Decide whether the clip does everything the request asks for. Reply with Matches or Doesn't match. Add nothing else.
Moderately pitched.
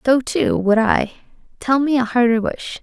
Doesn't match